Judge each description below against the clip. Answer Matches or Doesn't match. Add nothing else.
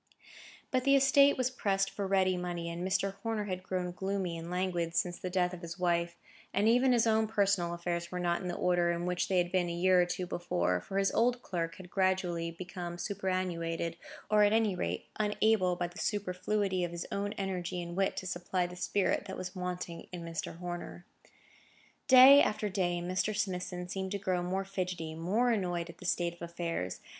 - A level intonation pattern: Matches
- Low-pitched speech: Doesn't match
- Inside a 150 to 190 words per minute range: Doesn't match